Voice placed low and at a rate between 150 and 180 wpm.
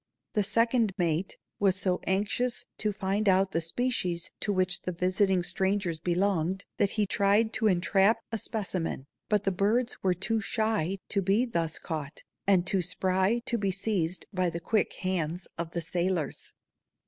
No: high, 190 Hz; average, 165 wpm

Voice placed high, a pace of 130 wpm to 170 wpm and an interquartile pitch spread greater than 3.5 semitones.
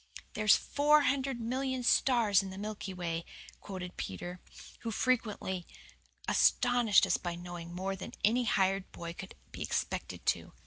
Yes: high, 200 Hz; average, 145 wpm; average, 5.3 semitones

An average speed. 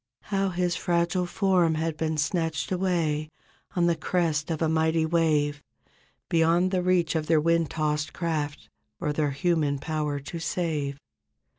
Yes: average, 150 wpm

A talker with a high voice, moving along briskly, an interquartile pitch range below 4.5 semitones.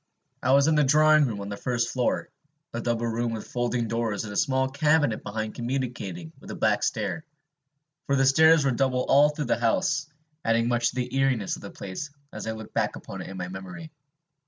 No: low, 120 Hz; fast, 215 wpm; average, 3.8 semitones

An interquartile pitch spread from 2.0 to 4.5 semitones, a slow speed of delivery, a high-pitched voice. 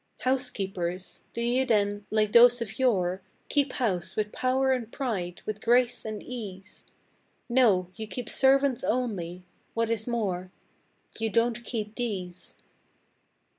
Yes: average, 4.1 semitones; slow, 130 wpm; high, 225 Hz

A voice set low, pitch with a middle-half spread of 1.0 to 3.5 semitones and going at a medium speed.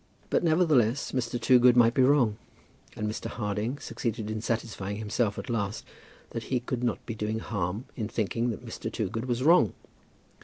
Yes: low, 115 Hz; average, 2.7 semitones; average, 170 wpm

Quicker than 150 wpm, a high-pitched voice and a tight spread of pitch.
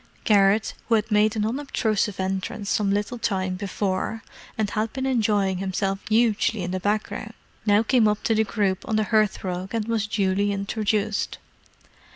Yes: average, 165 wpm; high, 210 Hz; narrow, 2.1 semitones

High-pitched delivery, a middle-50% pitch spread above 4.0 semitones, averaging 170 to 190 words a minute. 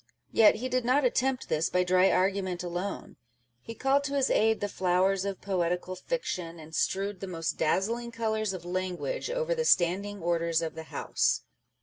Yes: high, 195 Hz; average, 4.6 semitones; average, 180 wpm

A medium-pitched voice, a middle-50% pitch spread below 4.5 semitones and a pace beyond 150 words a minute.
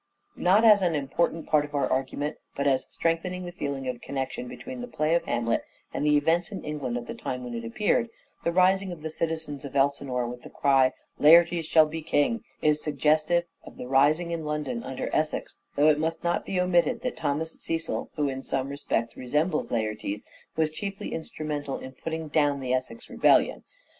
Yes: medium, 150 Hz; average, 3.9 semitones; average, 200 wpm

